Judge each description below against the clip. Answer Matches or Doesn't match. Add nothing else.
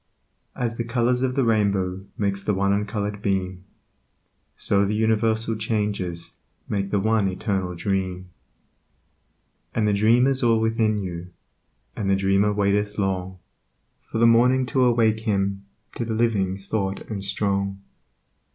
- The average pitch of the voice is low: Matches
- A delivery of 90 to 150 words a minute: Matches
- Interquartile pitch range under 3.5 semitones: Matches